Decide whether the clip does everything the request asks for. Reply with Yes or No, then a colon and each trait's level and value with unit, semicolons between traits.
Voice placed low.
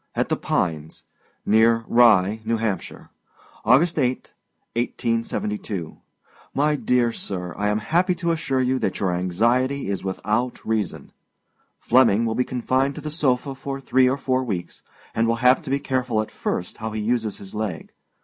Yes: low, 120 Hz